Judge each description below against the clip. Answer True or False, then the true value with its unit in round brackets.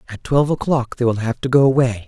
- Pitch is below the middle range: True (125 Hz)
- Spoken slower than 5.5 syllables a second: False (6.4 syllables/s)